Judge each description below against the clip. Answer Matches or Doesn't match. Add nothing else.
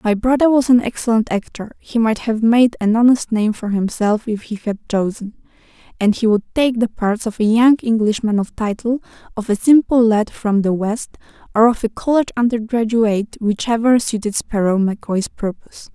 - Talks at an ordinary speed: Matches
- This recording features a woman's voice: Matches